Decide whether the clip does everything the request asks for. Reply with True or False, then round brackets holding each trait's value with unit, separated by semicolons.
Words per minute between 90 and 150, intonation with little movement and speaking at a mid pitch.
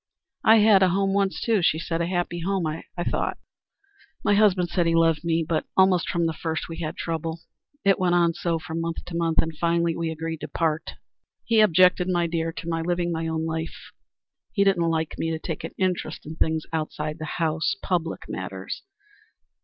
False (200 wpm; 1.8 semitones; 165 Hz)